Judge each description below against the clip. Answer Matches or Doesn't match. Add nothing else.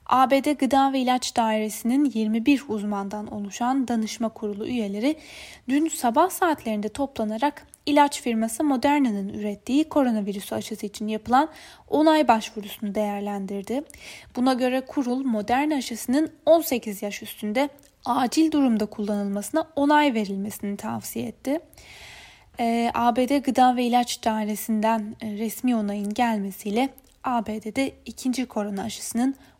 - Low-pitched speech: Doesn't match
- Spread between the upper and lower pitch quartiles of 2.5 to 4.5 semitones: Matches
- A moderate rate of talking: Matches